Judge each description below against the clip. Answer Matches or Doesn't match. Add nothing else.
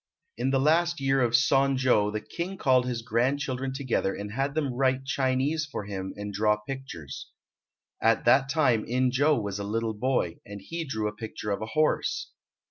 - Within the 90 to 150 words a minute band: Doesn't match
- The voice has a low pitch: Matches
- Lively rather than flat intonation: Doesn't match